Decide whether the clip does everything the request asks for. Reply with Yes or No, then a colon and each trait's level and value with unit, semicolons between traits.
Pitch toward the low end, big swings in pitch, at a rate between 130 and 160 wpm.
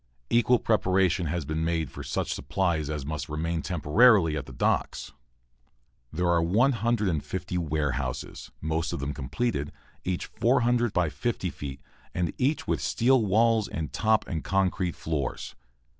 Yes: very low, 85 Hz; wide, 6.2 semitones; average, 145 wpm